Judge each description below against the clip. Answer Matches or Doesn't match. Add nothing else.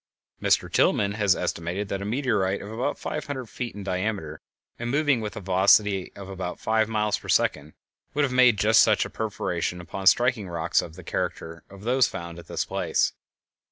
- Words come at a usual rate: Matches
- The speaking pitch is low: Matches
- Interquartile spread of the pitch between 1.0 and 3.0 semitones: Doesn't match